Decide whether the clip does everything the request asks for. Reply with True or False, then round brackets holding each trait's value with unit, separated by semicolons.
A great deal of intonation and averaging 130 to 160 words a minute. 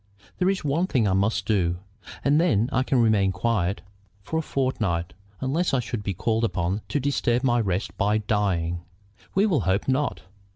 False (5.7 semitones; 180 wpm)